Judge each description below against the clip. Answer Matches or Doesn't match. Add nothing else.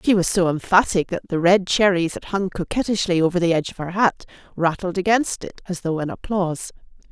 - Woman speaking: Matches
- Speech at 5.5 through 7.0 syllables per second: Matches